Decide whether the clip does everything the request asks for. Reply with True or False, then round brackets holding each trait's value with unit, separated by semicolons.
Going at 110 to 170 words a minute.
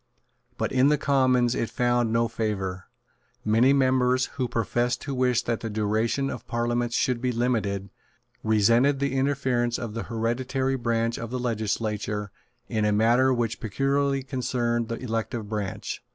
True (150 wpm)